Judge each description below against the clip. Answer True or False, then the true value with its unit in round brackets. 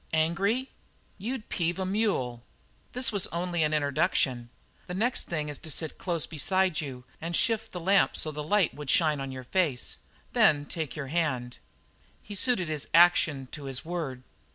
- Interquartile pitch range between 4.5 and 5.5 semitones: True (4.8 semitones)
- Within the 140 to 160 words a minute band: False (180 wpm)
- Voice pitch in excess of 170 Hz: False (160 Hz)